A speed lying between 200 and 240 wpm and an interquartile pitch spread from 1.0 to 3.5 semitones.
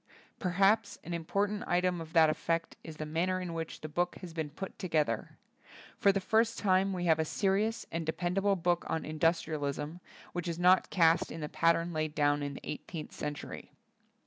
Yes: fast, 205 wpm; average, 2.9 semitones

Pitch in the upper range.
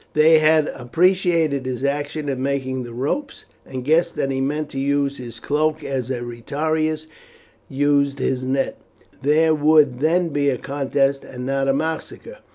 No: medium, 140 Hz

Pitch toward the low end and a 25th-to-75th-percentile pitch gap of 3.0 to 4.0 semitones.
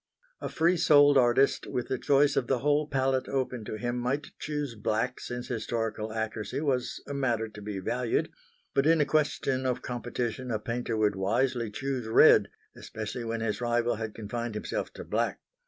Yes: low, 120 Hz; average, 3.3 semitones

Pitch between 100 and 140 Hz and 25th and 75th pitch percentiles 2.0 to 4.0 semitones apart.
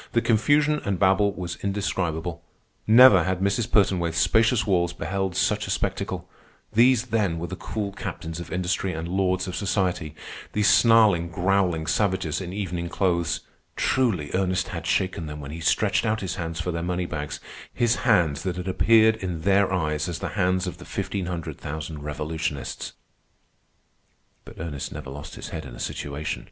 No: very low, 90 Hz; average, 3.4 semitones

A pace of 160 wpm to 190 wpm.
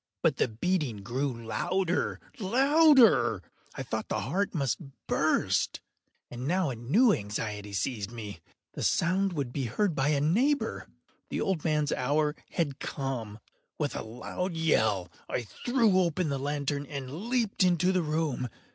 No: average, 145 wpm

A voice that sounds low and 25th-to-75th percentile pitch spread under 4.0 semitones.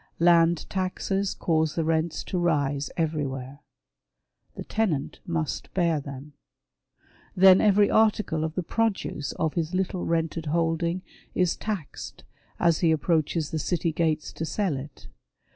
No: medium, 165 Hz; average, 2.9 semitones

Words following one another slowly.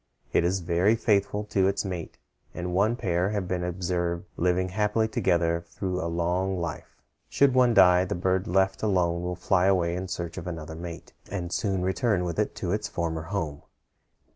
No: average, 185 wpm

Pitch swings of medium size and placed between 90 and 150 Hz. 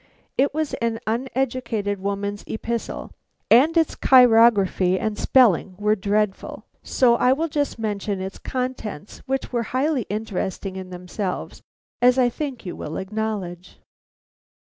No: average, 4.4 semitones; high, 220 Hz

